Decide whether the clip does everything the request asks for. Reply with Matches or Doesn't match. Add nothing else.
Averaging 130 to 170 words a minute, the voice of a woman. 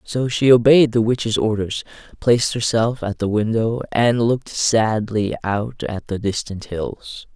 Doesn't match